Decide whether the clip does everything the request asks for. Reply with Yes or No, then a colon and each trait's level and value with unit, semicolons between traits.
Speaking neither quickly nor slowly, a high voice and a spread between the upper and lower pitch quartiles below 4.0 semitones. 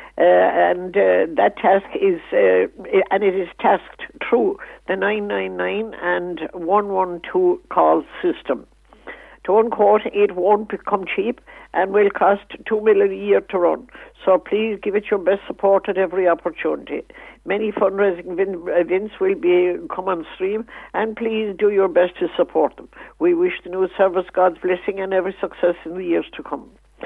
Yes: average, 165 wpm; high, 200 Hz; average, 3.2 semitones